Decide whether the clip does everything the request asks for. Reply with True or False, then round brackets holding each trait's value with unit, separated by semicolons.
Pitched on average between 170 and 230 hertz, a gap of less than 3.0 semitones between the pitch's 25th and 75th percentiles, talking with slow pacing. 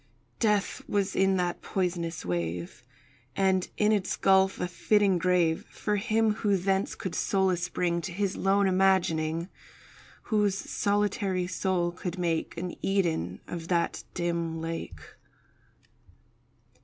True (185 Hz; 2.4 semitones; 125 wpm)